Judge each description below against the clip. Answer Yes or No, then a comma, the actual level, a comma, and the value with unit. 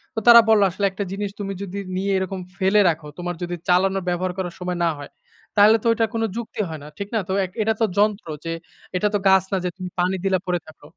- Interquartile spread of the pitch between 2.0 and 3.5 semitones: Yes, narrow, 2.5 semitones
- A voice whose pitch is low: No, high, 190 Hz